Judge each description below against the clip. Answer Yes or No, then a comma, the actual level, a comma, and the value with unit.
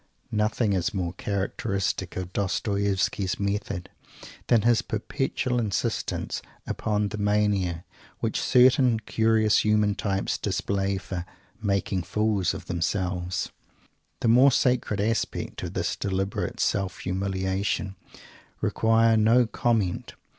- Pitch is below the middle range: Yes, low, 100 Hz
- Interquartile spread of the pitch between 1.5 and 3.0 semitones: Yes, average, 2.7 semitones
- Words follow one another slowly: Yes, slow, 110 wpm